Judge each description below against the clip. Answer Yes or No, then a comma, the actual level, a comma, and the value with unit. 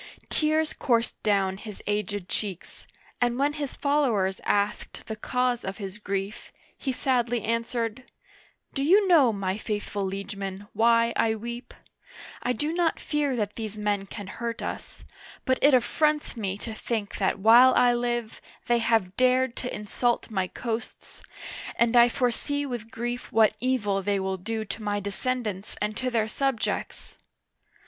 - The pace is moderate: Yes, average, 155 wpm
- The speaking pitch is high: Yes, high, 230 Hz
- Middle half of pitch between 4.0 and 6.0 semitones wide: No, average, 3.6 semitones